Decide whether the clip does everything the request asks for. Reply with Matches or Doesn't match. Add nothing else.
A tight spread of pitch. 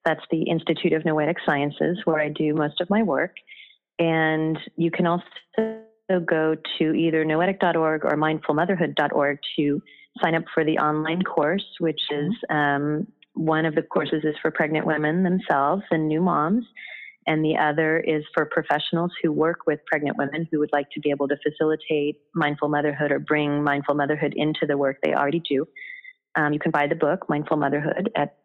Matches